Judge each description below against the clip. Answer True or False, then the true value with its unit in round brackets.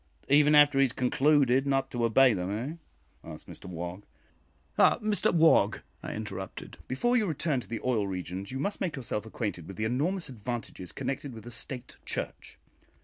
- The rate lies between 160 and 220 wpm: True (180 wpm)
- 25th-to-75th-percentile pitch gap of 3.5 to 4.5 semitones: False (5.1 semitones)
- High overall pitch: False (130 Hz)